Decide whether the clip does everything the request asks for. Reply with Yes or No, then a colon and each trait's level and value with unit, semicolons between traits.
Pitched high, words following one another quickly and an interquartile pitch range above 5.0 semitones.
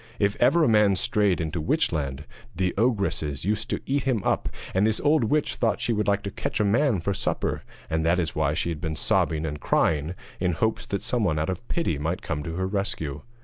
No: very low, 95 Hz; fast, 225 wpm; wide, 5.5 semitones